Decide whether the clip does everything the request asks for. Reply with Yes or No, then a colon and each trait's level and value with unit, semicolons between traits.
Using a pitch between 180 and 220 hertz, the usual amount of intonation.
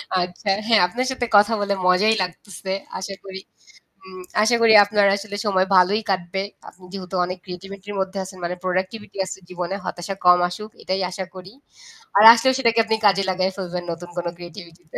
No: high, 190 Hz; narrow, 2.1 semitones